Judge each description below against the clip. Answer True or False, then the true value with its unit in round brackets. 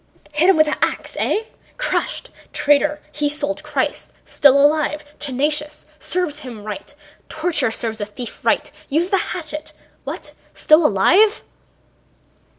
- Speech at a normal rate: False (130 wpm)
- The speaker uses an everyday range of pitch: False (1.9 semitones)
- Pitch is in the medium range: False (300 Hz)